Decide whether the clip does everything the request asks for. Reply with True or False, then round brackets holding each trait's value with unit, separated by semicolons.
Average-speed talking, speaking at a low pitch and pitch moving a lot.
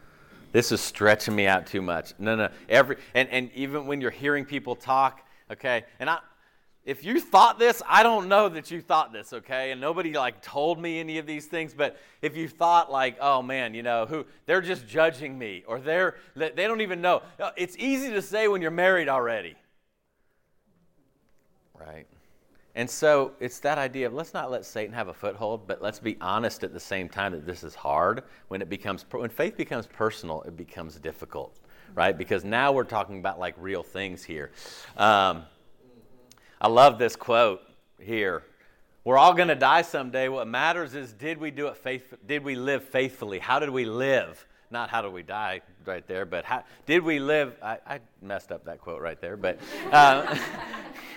True (195 wpm; 130 Hz; 6.7 semitones)